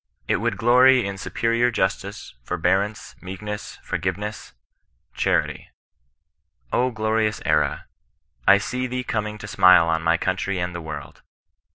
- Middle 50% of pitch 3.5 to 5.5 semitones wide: Yes, average, 3.9 semitones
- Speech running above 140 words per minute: No, slow, 135 wpm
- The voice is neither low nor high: No, low, 105 Hz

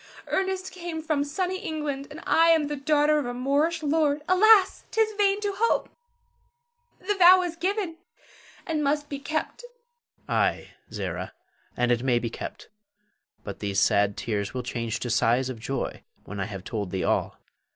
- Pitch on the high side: Yes, very high, 300 Hz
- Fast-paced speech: No, average, 170 wpm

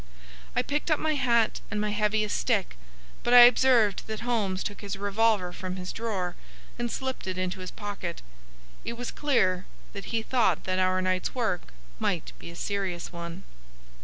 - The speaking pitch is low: No, high, 205 Hz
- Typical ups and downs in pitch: Yes, average, 4.0 semitones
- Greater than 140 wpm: Yes, average, 175 wpm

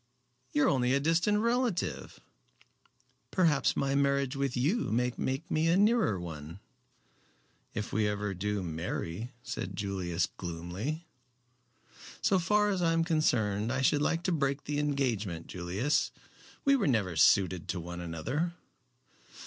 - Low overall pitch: Yes, low, 130 Hz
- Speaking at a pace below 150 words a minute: Yes, average, 140 wpm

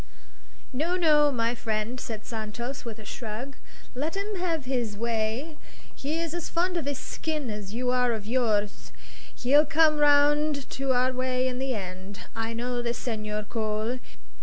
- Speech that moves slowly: No, average, 165 wpm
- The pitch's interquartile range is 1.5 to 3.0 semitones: No, average, 4.8 semitones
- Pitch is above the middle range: Yes, very high, 250 Hz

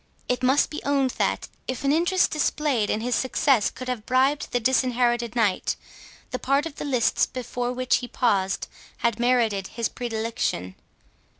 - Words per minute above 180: No, average, 165 wpm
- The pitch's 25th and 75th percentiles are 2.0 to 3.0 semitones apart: Yes, narrow, 2.5 semitones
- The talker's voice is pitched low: No, very high, 250 Hz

